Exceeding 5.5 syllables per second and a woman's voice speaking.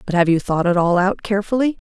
Yes: 6.5 syllables/s; female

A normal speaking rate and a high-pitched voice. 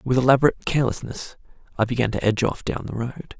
No: average, 195 wpm; low, 125 Hz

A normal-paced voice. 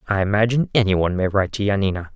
No: fast, 220 wpm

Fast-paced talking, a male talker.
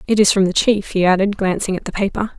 No: fast, 275 wpm; female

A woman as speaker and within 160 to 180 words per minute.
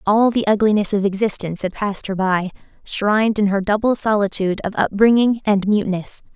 Yes: female; average, 170 wpm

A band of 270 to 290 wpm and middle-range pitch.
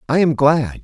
No: fast, 215 wpm; medium, 145 Hz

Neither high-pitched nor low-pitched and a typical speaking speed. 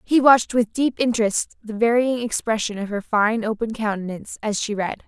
No: high, 220 Hz; average, 190 wpm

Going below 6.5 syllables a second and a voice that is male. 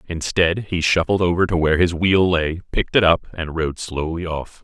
Yes: 5.1 syllables/s; male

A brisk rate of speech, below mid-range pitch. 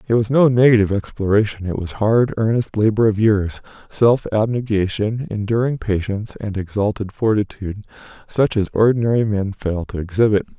No: average, 145 wpm; low, 105 Hz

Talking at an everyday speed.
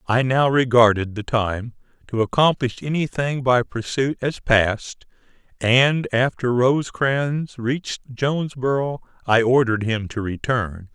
No: slow, 120 wpm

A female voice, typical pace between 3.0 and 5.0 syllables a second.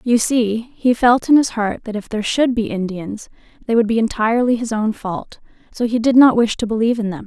No: female; 5.5 syllables/s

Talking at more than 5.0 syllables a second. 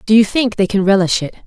Yes: 6.3 syllables/s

